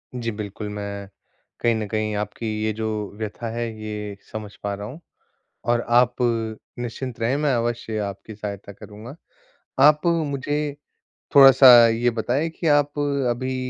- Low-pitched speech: Yes, low, 115 Hz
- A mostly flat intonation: No, average, 3.7 semitones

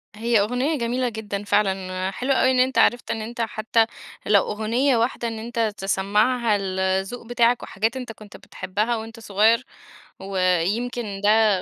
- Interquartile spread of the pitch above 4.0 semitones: No, average, 3.1 semitones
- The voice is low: No, high, 225 Hz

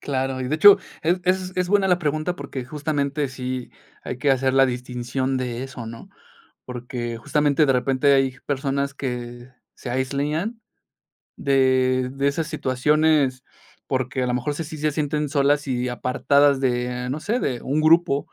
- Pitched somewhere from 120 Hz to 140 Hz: Yes, low, 135 Hz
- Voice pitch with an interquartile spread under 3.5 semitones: Yes, average, 2.8 semitones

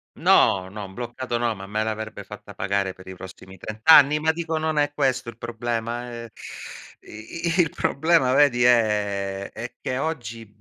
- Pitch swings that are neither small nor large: Yes, average, 5.0 semitones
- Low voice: Yes, low, 115 Hz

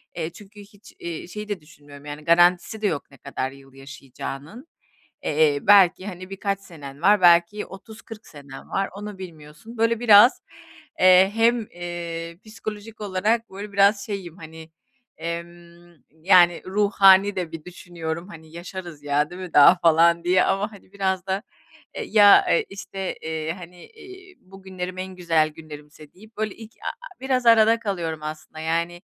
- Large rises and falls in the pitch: No, average, 4.0 semitones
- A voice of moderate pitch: Yes, medium, 180 Hz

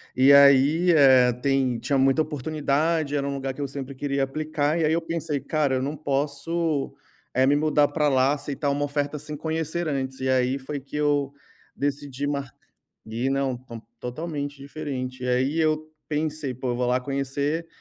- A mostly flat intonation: Yes, narrow, 2.3 semitones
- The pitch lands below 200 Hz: Yes, medium, 140 Hz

